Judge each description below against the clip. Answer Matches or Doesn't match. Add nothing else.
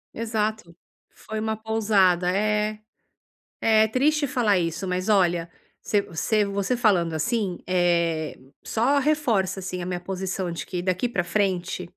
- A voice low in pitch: Doesn't match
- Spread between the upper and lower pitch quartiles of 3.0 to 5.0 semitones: Matches